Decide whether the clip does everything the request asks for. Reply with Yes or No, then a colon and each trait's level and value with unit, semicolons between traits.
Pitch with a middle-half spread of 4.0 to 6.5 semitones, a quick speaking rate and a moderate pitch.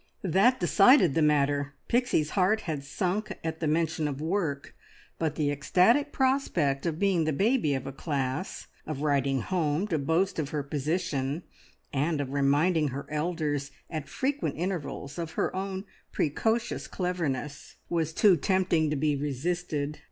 No: average, 4.3 semitones; average, 150 wpm; medium, 155 Hz